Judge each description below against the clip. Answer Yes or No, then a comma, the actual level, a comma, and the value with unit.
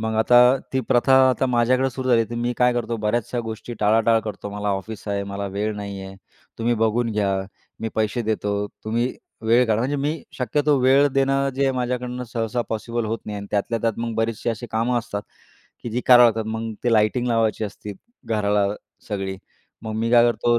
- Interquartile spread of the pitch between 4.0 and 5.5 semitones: No, narrow, 2.4 semitones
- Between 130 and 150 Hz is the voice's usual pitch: No, low, 115 Hz